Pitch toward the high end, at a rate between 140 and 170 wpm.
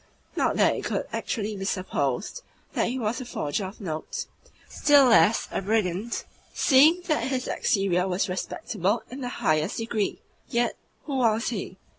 Yes: high, 220 Hz; average, 160 wpm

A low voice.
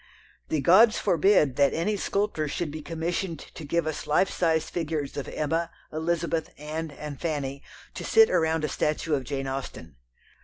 No: medium, 160 Hz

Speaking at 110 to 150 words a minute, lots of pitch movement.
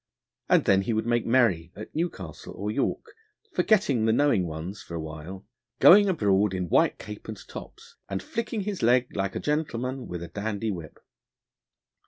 No: average, 175 wpm; wide, 5.8 semitones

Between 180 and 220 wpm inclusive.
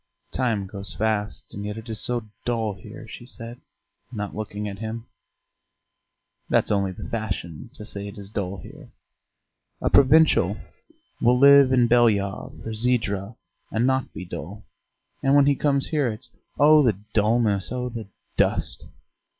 No: average, 155 wpm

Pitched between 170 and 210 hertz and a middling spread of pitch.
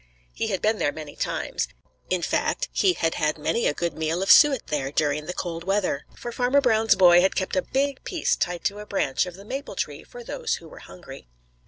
No: high, 190 Hz; wide, 7.2 semitones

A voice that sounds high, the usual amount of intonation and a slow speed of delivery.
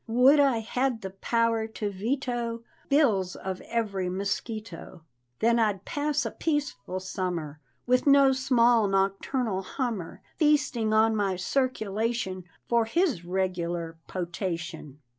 Yes: high, 220 Hz; average, 4.8 semitones; slow, 120 wpm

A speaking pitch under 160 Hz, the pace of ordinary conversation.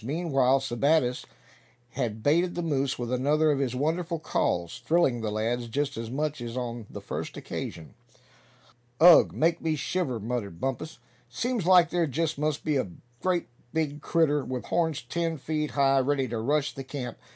Yes: medium, 140 Hz; average, 170 wpm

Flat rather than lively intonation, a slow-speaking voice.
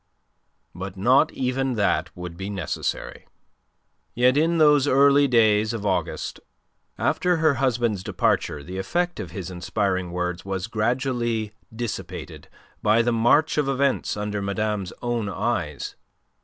No: average, 5.3 semitones; slow, 130 wpm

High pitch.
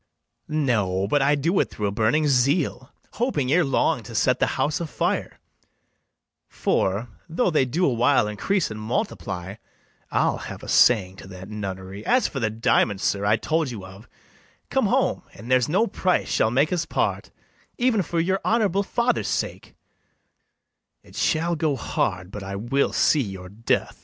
No: low, 130 Hz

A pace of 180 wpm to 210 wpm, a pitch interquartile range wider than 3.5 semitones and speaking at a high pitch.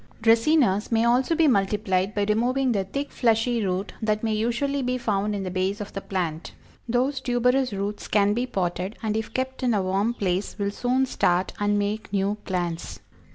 Yes: average, 190 wpm; average, 4.0 semitones; high, 215 Hz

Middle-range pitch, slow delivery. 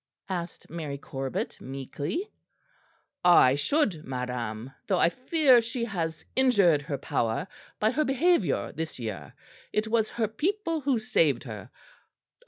Yes: medium, 175 Hz; slow, 130 wpm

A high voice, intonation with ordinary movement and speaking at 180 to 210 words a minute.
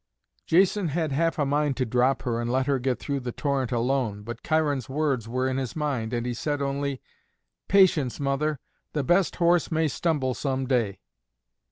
No: low, 135 Hz; average, 3.4 semitones; average, 185 wpm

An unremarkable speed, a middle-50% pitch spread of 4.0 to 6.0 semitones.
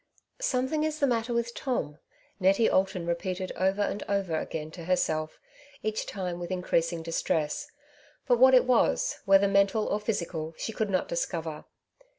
Yes: average, 165 wpm; average, 5.0 semitones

